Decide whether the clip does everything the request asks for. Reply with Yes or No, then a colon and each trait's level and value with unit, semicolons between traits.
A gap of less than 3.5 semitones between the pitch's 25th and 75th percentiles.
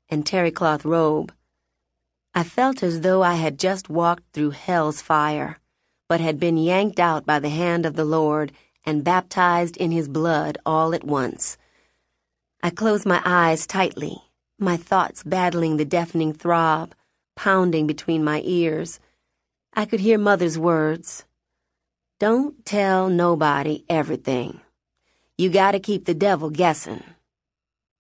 Yes: average, 3.0 semitones